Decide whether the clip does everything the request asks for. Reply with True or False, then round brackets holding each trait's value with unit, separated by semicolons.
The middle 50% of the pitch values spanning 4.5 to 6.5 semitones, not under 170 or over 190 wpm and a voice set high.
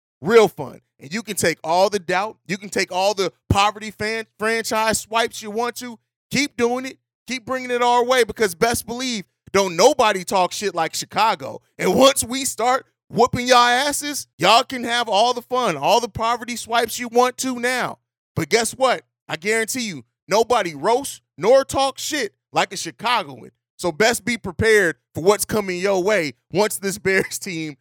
True (5.1 semitones; 185 wpm; 220 Hz)